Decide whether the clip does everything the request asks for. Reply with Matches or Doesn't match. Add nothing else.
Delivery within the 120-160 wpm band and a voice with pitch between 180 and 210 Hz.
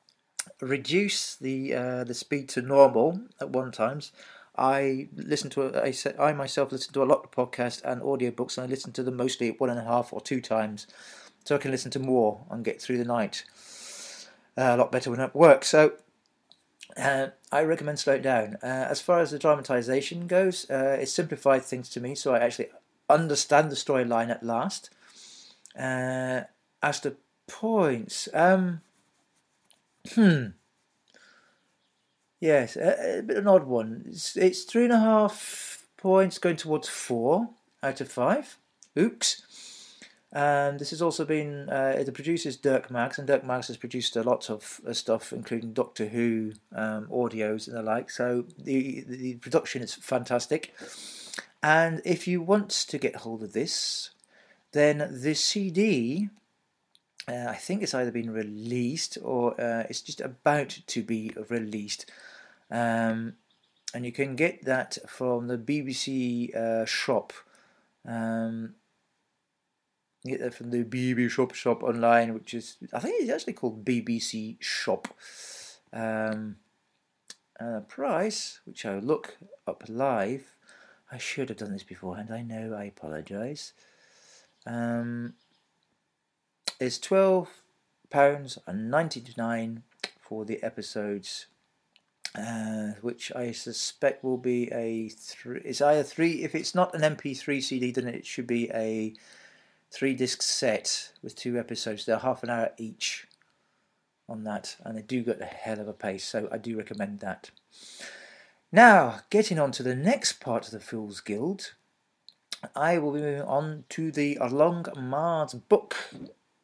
Doesn't match